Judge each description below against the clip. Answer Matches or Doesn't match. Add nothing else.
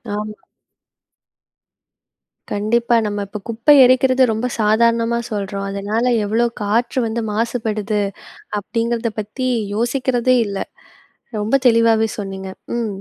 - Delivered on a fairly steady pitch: Matches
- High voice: Matches